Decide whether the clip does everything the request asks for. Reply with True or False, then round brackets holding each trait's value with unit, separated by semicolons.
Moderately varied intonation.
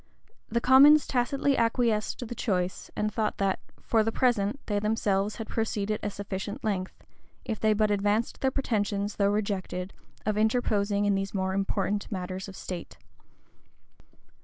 False (2.1 semitones)